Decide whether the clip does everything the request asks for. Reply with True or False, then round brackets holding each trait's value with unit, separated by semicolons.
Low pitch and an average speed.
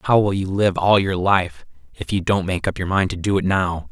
False (95 Hz; 275 wpm)